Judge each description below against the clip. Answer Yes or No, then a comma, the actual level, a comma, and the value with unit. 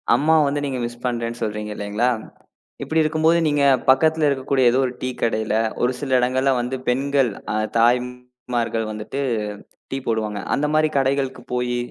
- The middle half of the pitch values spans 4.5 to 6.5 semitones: No, average, 2.8 semitones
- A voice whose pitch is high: No, low, 125 Hz